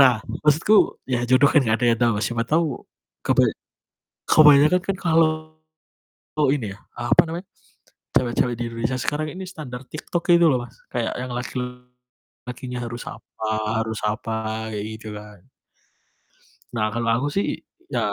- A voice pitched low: Yes, low, 125 Hz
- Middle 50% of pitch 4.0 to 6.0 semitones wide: Yes, average, 5.0 semitones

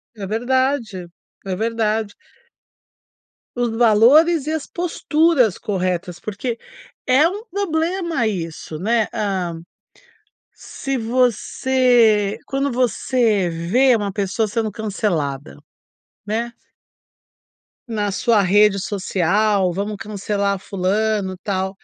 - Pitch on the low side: No, high, 215 Hz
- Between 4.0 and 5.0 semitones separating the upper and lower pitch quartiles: Yes, average, 4.4 semitones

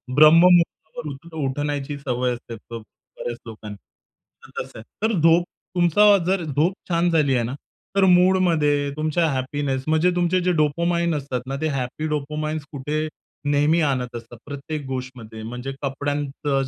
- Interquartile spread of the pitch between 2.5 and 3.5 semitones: No, average, 3.9 semitones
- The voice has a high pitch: No, medium, 145 Hz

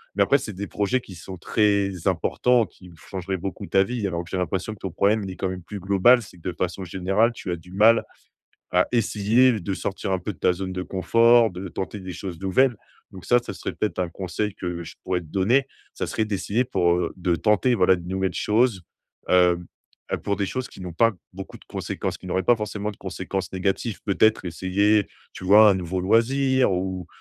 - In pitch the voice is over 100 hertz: No, very low, 95 Hz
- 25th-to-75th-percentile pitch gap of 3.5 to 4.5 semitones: No, average, 2.9 semitones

